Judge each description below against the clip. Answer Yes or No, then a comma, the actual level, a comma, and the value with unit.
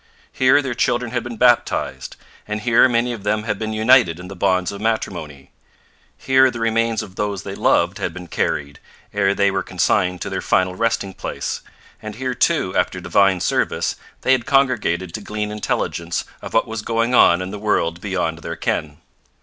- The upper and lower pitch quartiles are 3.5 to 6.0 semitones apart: Yes, average, 4.2 semitones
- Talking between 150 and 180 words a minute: No, average, 190 wpm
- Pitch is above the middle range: No, low, 105 Hz